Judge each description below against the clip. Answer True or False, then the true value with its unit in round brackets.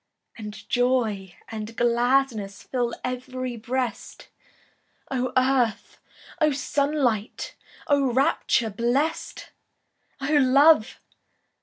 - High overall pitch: True (250 Hz)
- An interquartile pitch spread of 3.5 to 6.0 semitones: False (3.0 semitones)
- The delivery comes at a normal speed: False (85 wpm)